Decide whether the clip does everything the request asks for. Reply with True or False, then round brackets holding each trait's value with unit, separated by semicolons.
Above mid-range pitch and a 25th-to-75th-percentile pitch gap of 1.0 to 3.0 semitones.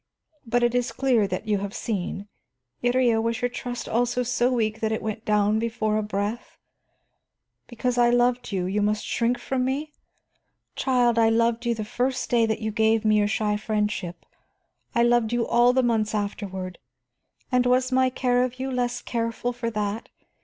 True (230 Hz; 2.4 semitones)